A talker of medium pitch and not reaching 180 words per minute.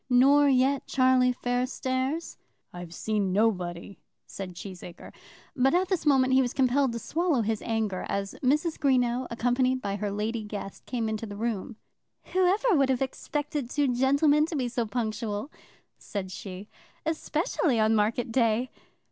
No: high, 245 Hz; average, 150 wpm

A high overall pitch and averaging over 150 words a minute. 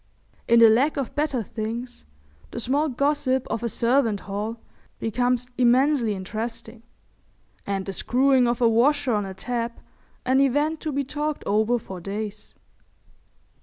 No: high, 240 Hz; average, 145 wpm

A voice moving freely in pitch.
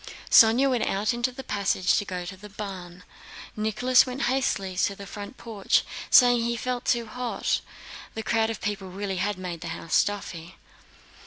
No: average, 3.9 semitones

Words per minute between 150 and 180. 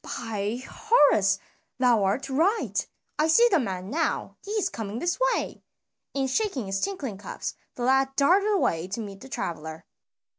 Yes: average, 160 wpm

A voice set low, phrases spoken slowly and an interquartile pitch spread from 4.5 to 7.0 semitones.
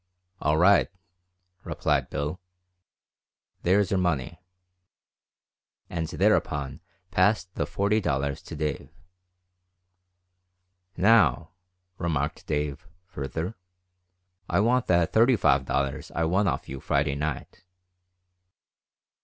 Yes: very low, 85 Hz; slow, 95 wpm; average, 5.3 semitones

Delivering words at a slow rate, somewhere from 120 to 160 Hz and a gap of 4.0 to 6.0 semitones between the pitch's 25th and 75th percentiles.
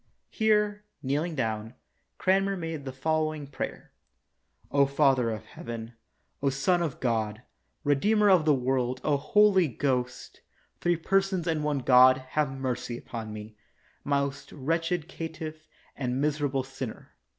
Yes: slow, 130 wpm; medium, 140 Hz; average, 4.3 semitones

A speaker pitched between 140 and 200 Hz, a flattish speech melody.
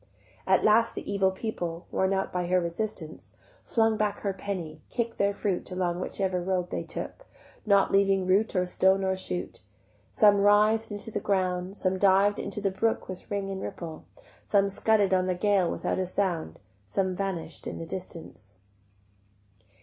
Yes: high, 190 Hz; narrow, 1.9 semitones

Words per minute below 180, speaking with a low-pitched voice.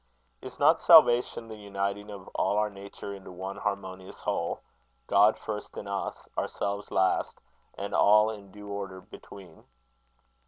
Yes: average, 145 wpm; low, 100 Hz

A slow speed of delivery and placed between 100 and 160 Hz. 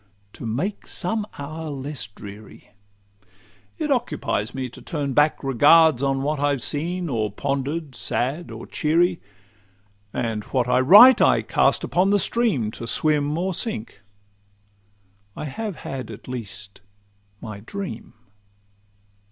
Yes: slow, 125 wpm; medium, 140 Hz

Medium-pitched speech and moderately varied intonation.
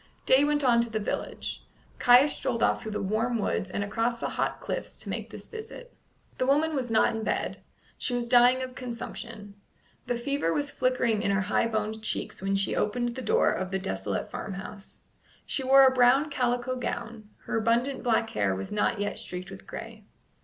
No: high, 235 Hz; average, 3.6 semitones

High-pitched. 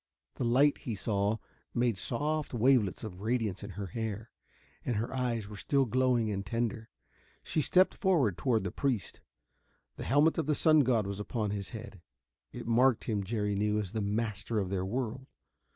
No: low, 115 Hz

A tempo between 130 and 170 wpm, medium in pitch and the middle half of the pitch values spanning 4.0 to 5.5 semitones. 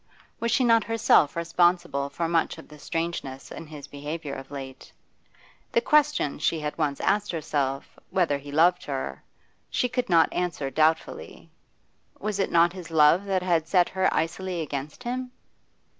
Yes: average, 160 wpm; medium, 165 Hz; average, 4.3 semitones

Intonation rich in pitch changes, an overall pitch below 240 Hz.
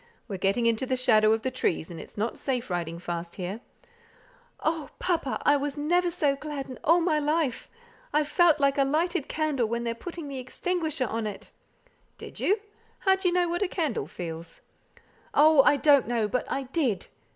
No: wide, 5.8 semitones; very high, 275 Hz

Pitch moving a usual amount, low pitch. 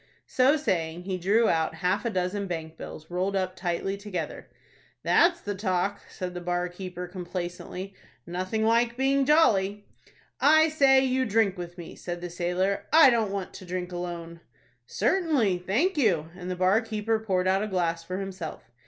No: average, 3.8 semitones; high, 190 Hz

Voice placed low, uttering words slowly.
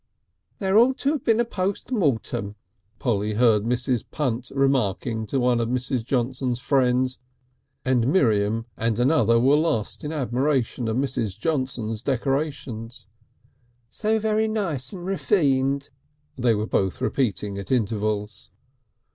Yes: low, 125 Hz; slow, 130 wpm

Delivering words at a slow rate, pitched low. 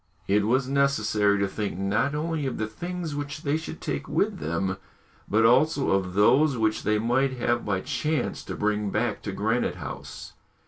No: average, 180 wpm; low, 115 Hz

